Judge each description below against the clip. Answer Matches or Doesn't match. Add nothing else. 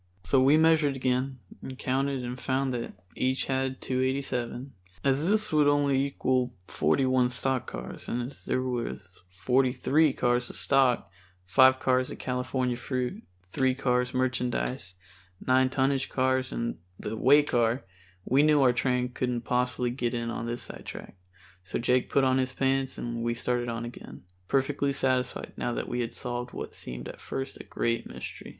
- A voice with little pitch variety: Matches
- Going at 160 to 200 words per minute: Matches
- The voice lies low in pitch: Matches